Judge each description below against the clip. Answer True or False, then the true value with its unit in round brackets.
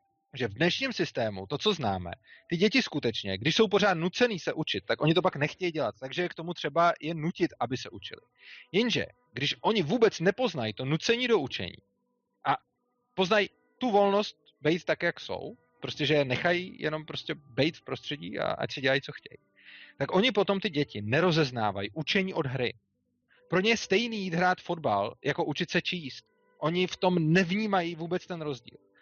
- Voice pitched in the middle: True (170 Hz)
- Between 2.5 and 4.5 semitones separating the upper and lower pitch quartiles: False (5.2 semitones)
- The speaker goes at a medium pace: False (185 wpm)